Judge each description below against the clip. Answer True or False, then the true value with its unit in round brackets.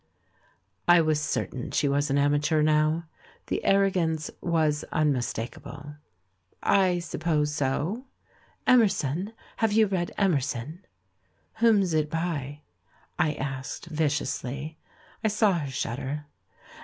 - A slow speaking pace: True (110 wpm)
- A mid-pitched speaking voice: True (155 Hz)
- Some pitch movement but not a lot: True (3.6 semitones)